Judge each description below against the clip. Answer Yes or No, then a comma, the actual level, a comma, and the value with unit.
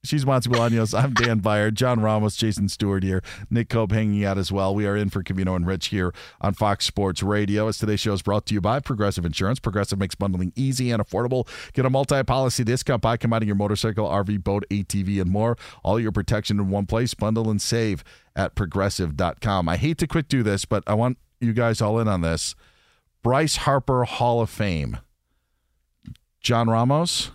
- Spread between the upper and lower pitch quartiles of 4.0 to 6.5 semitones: No, average, 3.1 semitones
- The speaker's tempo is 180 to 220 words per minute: Yes, average, 200 wpm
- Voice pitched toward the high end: No, low, 105 Hz